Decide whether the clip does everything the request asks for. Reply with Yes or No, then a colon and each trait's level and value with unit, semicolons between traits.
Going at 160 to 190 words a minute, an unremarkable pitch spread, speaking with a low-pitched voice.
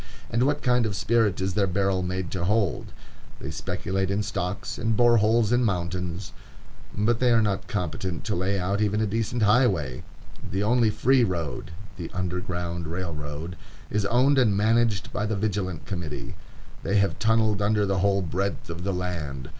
Yes: average, 175 wpm; average, 3.4 semitones; low, 100 Hz